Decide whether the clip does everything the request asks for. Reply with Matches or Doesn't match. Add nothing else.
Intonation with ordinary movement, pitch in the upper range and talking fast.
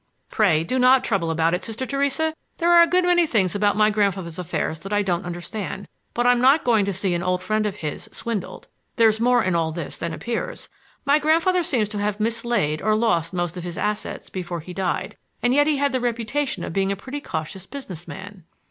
Doesn't match